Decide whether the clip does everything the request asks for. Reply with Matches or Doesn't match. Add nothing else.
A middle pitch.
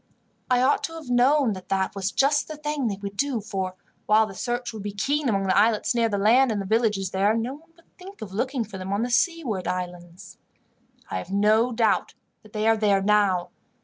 Doesn't match